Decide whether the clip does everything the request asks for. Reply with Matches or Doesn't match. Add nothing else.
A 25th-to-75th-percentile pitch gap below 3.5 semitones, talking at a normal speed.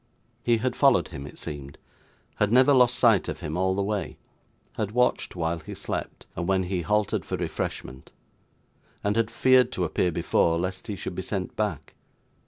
Doesn't match